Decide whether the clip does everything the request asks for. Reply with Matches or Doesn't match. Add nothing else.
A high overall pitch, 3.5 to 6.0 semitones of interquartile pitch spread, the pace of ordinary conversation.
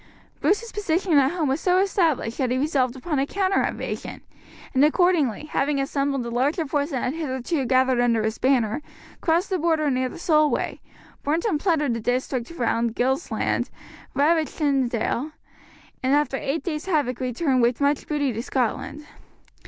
Matches